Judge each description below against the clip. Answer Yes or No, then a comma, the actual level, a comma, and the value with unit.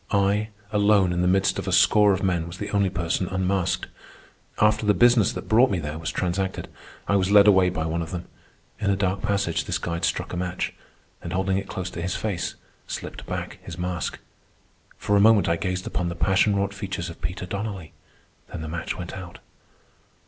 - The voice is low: Yes, very low, 95 Hz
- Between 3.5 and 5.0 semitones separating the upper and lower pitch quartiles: No, narrow, 2.4 semitones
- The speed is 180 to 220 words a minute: Yes, fast, 205 wpm